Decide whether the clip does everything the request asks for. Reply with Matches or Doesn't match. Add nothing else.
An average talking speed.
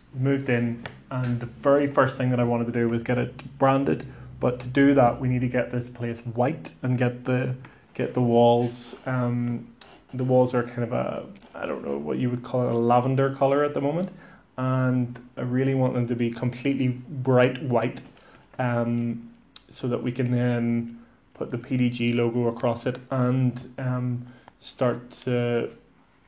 Matches